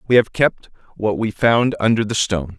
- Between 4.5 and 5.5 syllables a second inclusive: Yes, 5.3 syllables/s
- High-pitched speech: No, low, 105 Hz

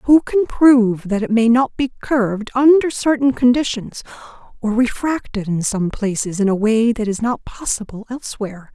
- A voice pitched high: Yes, high, 235 Hz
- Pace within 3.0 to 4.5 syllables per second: No, 4.9 syllables/s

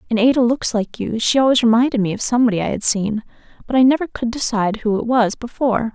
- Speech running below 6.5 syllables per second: No, 6.6 syllables/s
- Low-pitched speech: No, high, 235 Hz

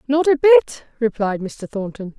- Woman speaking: Yes, female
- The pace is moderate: Yes, average, 165 wpm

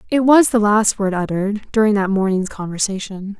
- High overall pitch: Yes, high, 205 Hz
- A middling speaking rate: Yes, average, 175 wpm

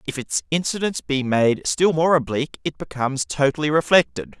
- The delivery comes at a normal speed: Yes, average, 165 wpm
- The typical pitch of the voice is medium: Yes, medium, 145 Hz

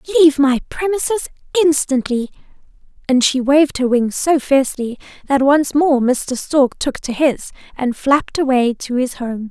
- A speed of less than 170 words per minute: Yes, average, 160 wpm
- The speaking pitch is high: Yes, very high, 275 Hz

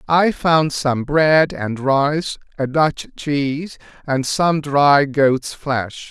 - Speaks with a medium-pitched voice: Yes, medium, 145 Hz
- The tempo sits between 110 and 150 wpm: Yes, average, 140 wpm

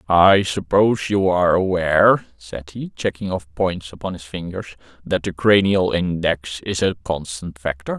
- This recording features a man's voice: Yes, male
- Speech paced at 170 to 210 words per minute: No, average, 160 wpm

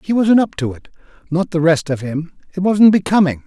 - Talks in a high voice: No, medium, 170 Hz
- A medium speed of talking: No, fast, 210 wpm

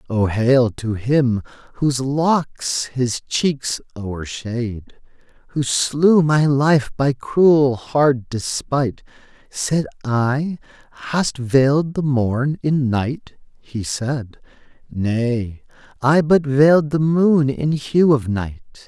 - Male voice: Yes, male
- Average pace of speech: No, slow, 120 wpm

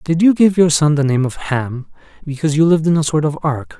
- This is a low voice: No, medium, 155 Hz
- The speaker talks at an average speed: No, fast, 270 wpm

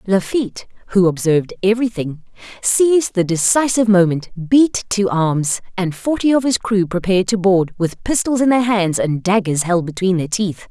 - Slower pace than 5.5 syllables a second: Yes, 5.0 syllables/s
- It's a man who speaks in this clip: No, female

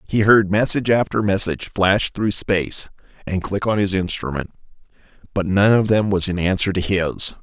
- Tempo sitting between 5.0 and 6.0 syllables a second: Yes, 5.1 syllables/s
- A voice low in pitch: Yes, low, 100 Hz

